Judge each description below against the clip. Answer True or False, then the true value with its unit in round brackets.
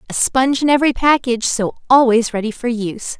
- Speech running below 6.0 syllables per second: False (6.3 syllables/s)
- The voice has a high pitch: True (245 Hz)